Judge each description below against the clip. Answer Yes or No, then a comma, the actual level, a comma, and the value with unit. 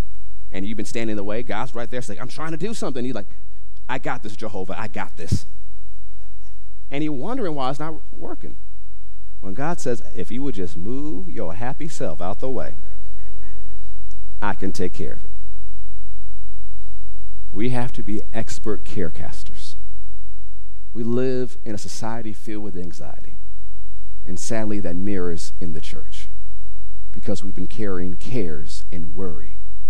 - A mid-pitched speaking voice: No, very low, 95 Hz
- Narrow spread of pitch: Yes, narrow, 2.3 semitones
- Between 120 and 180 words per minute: Yes, average, 160 wpm